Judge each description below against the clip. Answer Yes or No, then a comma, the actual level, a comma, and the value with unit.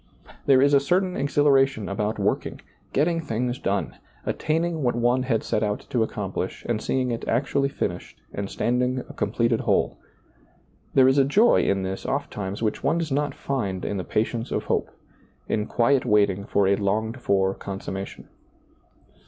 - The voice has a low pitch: Yes, low, 120 Hz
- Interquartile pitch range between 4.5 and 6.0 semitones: Yes, average, 5.1 semitones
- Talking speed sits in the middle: Yes, average, 165 wpm